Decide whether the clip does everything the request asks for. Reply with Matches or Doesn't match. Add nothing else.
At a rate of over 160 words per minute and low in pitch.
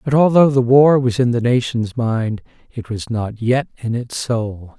Matches